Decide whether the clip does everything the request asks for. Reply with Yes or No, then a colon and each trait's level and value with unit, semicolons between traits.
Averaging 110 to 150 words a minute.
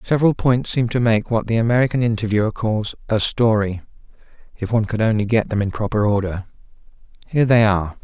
No: average, 180 wpm